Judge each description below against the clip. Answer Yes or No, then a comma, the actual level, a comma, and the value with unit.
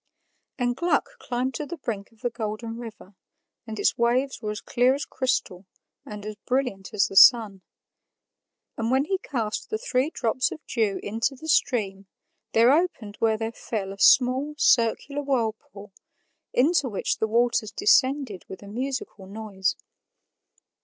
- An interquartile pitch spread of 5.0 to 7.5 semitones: No, average, 4.0 semitones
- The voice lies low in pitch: No, high, 235 Hz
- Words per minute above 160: No, average, 155 wpm